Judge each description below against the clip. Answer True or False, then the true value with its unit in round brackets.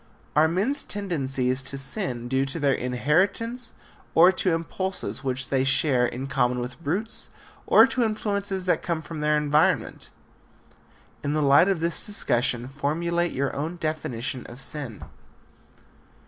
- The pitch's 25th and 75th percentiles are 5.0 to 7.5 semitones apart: True (5.4 semitones)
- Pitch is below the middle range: False (150 Hz)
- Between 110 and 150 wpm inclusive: True (145 wpm)